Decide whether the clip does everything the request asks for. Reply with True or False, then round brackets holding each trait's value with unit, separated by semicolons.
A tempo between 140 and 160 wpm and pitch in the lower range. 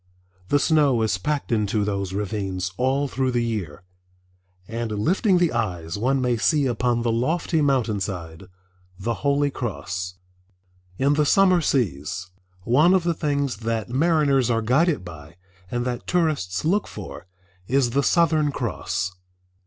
True (145 wpm; 120 Hz)